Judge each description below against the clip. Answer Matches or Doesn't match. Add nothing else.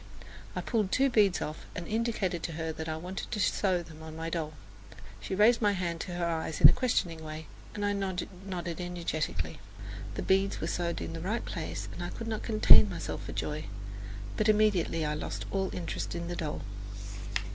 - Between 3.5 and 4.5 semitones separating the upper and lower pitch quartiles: Matches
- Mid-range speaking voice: Matches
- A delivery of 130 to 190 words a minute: Doesn't match